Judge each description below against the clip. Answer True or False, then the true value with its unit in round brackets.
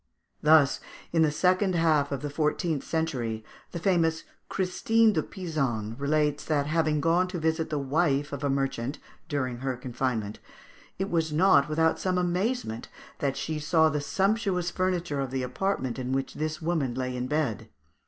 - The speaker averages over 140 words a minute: True (170 wpm)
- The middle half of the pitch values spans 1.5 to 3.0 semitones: False (4.2 semitones)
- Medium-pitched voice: True (155 Hz)